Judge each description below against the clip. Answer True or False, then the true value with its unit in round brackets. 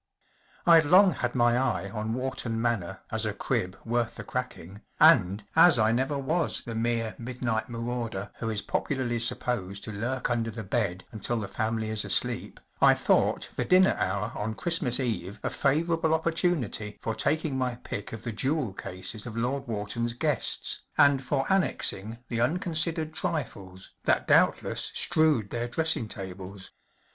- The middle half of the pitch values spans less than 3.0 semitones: False (4.3 semitones)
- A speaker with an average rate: True (160 wpm)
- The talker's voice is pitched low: True (120 Hz)